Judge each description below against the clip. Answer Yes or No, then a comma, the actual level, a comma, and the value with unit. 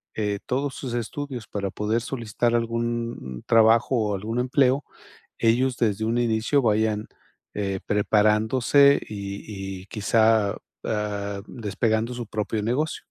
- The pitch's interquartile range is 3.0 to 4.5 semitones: No, narrow, 2.5 semitones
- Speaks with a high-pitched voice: No, low, 110 Hz